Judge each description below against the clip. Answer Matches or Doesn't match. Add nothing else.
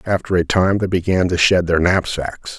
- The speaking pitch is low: Matches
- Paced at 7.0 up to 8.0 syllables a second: Doesn't match